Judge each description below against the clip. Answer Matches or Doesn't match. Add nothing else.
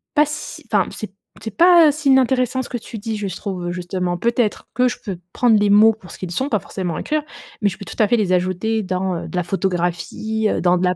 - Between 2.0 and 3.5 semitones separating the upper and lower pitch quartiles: Doesn't match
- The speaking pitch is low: Doesn't match